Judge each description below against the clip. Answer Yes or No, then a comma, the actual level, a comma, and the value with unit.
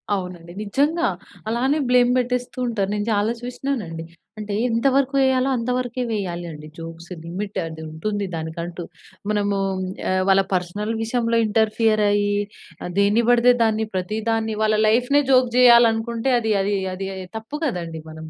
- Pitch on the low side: No, high, 215 Hz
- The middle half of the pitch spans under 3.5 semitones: No, average, 4.2 semitones